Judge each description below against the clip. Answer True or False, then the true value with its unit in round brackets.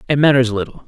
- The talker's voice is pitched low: True (130 Hz)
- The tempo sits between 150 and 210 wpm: True (205 wpm)